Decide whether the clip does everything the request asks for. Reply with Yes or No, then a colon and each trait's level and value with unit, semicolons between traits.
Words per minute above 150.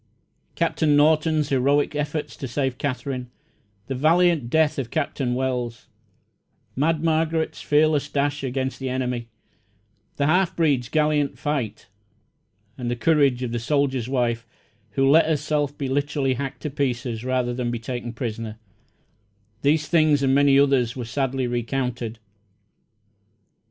No: slow, 135 wpm